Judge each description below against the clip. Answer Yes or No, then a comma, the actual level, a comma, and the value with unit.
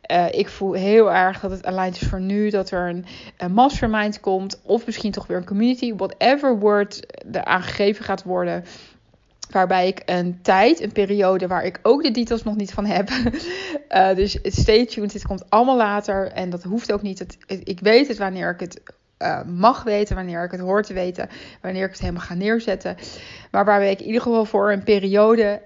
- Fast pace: Yes, fast, 205 wpm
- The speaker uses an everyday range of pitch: Yes, average, 3.0 semitones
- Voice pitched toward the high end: Yes, high, 205 Hz